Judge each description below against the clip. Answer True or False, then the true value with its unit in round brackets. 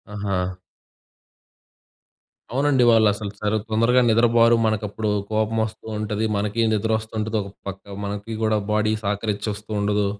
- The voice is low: True (110 Hz)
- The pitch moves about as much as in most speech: False (1.4 semitones)